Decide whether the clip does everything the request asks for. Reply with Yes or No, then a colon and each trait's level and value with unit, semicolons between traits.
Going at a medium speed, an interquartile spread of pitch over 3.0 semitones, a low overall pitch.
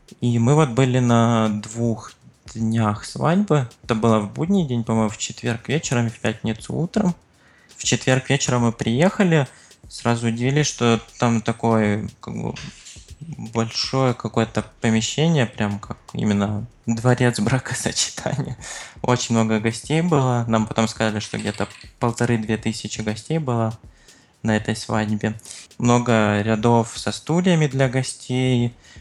No: average, 130 wpm; average, 2.7 semitones; low, 115 Hz